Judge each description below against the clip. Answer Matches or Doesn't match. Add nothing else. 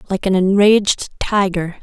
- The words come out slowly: Matches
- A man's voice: Doesn't match